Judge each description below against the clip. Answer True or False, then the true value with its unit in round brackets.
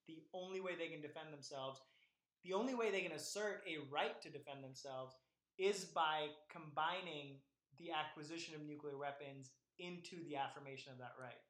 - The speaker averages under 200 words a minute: True (165 wpm)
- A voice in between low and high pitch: True (155 Hz)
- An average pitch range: True (3.8 semitones)